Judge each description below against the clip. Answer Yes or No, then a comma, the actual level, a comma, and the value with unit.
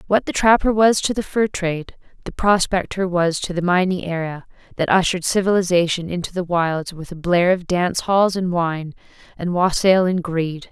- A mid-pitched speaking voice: Yes, medium, 180 Hz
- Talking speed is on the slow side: No, average, 185 wpm